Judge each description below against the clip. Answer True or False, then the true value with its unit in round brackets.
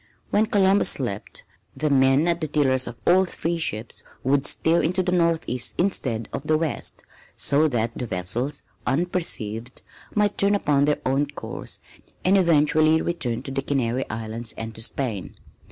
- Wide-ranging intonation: True (5.9 semitones)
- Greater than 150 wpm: True (160 wpm)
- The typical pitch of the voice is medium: True (145 Hz)